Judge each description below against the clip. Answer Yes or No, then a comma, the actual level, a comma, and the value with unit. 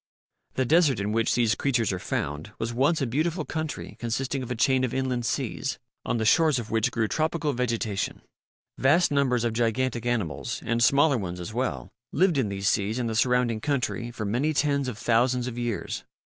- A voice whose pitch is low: Yes, low, 120 Hz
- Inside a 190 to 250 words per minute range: Yes, average, 195 wpm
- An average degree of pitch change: Yes, average, 3.5 semitones